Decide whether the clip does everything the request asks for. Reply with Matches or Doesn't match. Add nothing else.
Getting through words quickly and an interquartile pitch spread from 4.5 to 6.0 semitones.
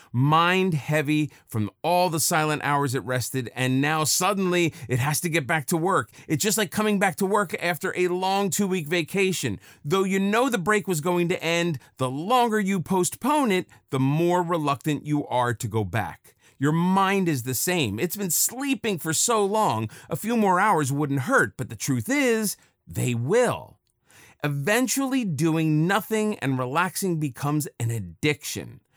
Doesn't match